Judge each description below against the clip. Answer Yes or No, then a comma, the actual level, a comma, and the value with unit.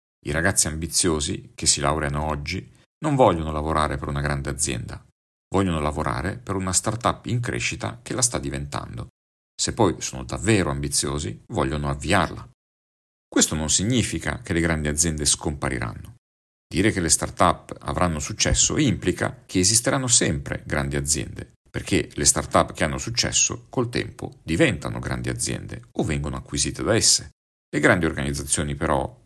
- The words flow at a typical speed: Yes, average, 150 wpm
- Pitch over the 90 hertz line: No, very low, 75 Hz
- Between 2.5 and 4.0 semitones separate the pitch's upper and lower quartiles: No, average, 5.0 semitones